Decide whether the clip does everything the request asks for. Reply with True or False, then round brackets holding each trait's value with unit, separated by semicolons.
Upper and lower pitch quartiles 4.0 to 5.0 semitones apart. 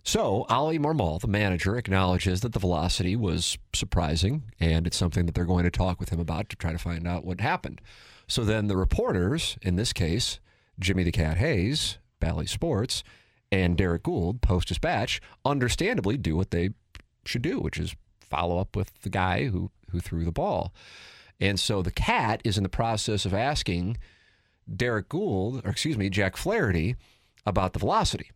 False (3.3 semitones)